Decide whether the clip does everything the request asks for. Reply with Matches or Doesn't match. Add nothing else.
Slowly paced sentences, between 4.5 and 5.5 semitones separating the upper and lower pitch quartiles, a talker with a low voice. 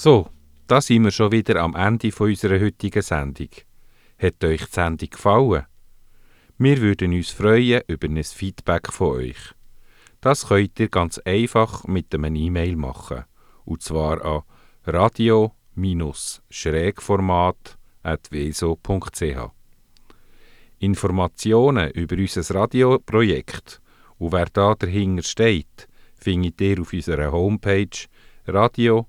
Matches